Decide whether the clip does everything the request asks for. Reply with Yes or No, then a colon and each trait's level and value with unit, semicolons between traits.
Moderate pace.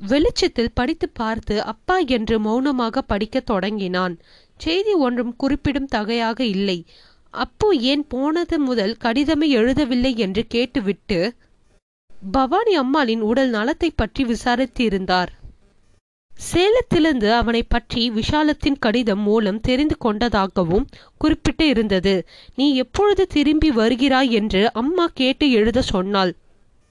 Yes: average, 105 wpm